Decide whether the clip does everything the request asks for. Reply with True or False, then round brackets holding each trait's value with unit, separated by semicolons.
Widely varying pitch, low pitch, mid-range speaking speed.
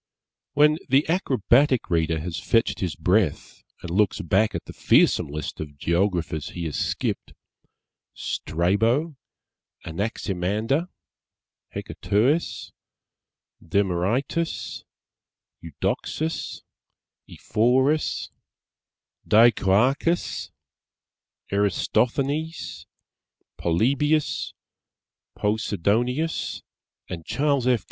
False (7.8 semitones; 110 Hz; 70 wpm)